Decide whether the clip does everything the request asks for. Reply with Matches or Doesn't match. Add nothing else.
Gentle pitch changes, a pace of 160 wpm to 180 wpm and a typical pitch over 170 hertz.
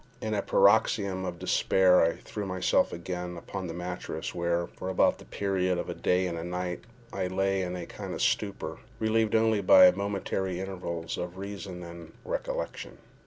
Doesn't match